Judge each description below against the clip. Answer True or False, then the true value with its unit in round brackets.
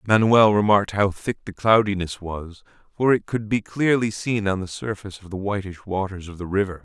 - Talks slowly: False (200 wpm)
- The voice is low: True (100 Hz)